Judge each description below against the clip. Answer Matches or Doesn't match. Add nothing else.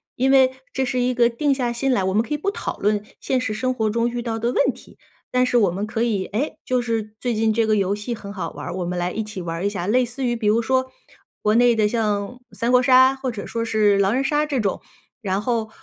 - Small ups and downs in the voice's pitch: Doesn't match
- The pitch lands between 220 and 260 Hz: Matches